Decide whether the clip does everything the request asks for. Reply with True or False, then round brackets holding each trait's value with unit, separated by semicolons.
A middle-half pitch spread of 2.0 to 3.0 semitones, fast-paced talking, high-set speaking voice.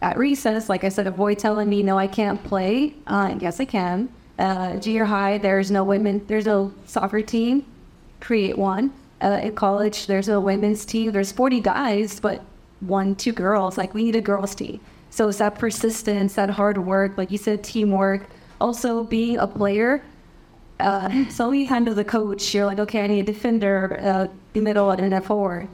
True (2.4 semitones; 195 wpm; 205 Hz)